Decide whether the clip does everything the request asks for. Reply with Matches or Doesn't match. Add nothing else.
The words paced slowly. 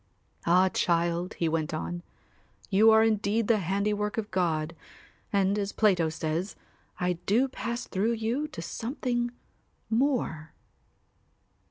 Matches